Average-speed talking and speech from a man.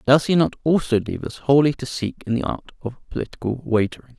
No: fast, 215 wpm; male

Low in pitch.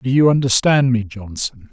Yes: low, 120 Hz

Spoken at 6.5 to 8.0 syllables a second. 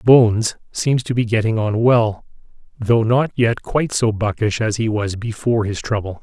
No: 4.8 syllables/s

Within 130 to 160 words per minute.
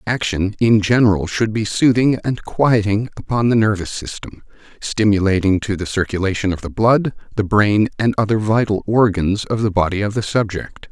No: average, 175 wpm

